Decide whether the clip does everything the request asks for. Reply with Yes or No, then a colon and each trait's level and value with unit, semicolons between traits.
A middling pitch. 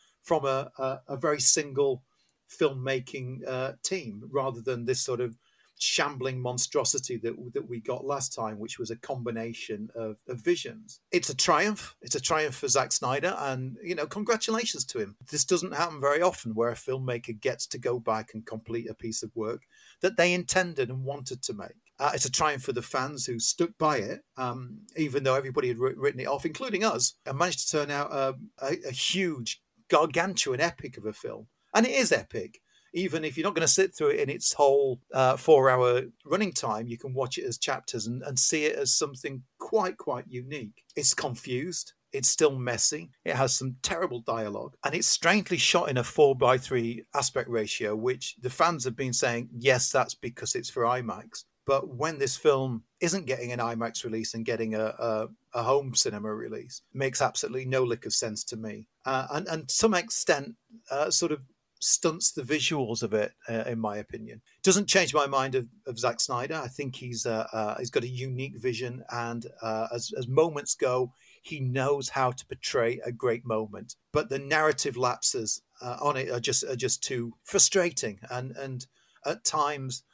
No: low, 130 Hz